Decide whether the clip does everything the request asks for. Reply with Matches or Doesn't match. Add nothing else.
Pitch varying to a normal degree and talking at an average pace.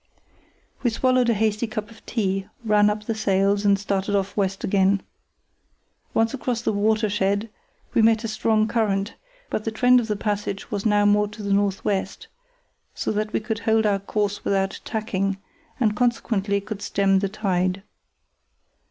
Doesn't match